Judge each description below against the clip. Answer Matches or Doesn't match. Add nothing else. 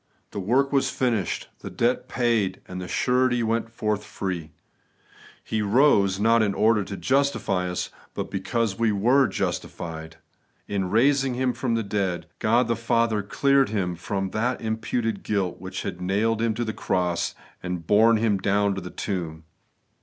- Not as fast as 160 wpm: Doesn't match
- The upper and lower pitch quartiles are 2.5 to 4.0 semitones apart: Matches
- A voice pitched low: Matches